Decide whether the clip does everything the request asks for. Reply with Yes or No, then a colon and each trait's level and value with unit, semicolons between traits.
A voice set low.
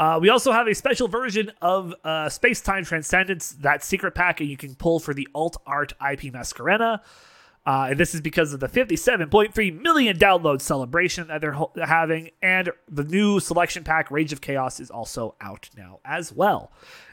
No: medium, 165 Hz